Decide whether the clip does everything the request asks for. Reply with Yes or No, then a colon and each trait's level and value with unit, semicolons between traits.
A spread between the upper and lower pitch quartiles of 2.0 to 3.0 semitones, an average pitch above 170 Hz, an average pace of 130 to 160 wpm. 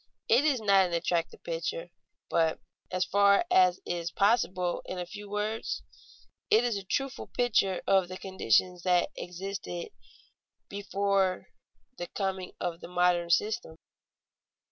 Yes: narrow, 2.4 semitones; medium, 185 Hz; slow, 135 wpm